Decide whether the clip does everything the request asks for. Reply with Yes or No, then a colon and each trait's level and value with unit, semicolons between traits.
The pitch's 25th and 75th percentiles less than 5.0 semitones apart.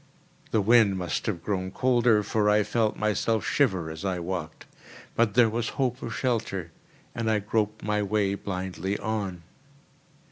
Yes: average, 3.1 semitones